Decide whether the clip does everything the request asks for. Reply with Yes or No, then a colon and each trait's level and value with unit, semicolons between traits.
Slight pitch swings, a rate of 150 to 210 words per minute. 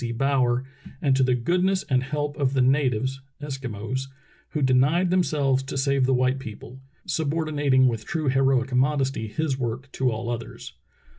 Yes: narrow, 2.2 semitones; average, 160 wpm